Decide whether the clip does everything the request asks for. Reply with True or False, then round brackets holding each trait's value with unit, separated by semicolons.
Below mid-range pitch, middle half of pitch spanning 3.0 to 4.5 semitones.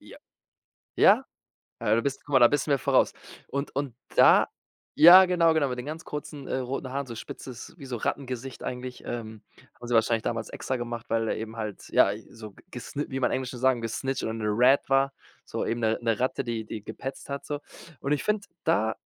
True (130 Hz; 3.4 semitones)